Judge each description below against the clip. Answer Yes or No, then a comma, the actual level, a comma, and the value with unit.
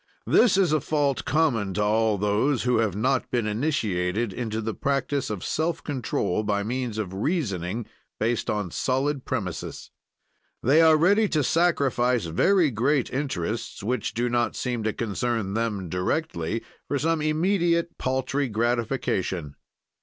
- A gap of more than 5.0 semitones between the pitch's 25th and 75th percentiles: Yes, wide, 5.6 semitones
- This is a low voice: Yes, low, 120 Hz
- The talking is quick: No, average, 145 wpm